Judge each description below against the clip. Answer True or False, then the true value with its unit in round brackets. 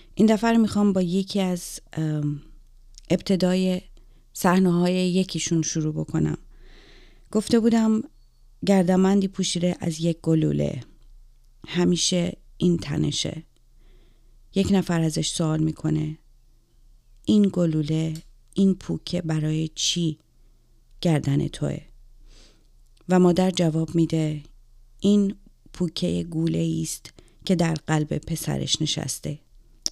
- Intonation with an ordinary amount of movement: False (6.7 semitones)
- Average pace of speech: False (100 wpm)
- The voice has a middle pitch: True (160 Hz)